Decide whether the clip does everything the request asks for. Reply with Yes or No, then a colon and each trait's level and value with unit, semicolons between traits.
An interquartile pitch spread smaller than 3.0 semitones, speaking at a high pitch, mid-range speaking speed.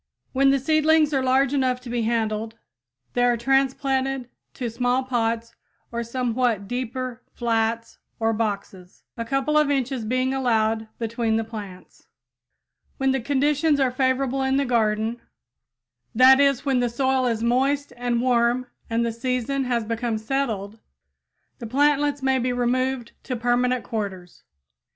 Yes: narrow, 2.6 semitones; high, 245 Hz; average, 145 wpm